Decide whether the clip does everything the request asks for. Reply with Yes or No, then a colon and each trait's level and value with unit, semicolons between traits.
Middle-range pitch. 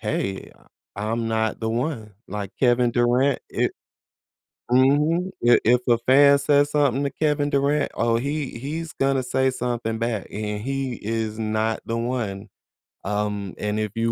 No: low, 120 Hz